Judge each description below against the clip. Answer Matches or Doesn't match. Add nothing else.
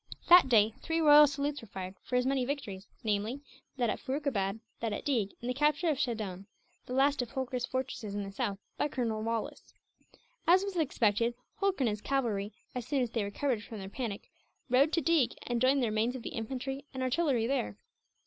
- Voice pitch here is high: Matches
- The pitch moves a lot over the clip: Doesn't match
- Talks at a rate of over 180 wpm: Matches